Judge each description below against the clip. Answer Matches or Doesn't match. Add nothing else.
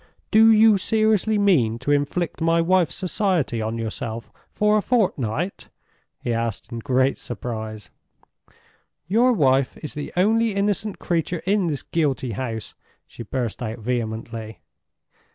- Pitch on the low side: Doesn't match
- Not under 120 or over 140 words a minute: Matches